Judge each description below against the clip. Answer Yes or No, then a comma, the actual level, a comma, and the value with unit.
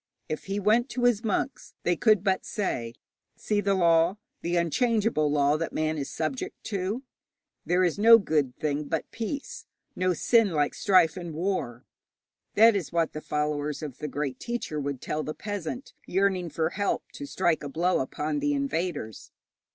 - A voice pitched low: No, medium, 175 Hz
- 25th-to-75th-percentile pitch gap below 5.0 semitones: No, wide, 5.4 semitones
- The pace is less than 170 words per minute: No, average, 175 wpm